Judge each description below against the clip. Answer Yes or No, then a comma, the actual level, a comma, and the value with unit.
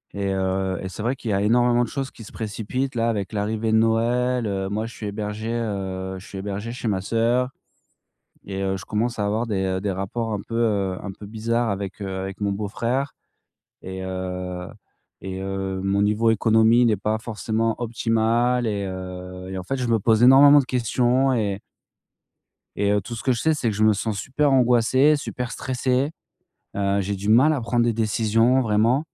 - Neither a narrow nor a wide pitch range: Yes, average, 3.4 semitones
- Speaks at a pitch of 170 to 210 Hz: No, low, 110 Hz